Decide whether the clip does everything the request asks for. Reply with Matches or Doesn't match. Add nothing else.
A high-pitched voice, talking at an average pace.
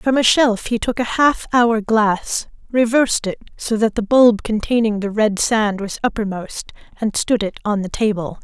Matches